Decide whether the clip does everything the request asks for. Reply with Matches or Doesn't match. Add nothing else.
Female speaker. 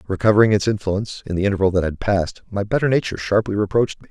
Doesn't match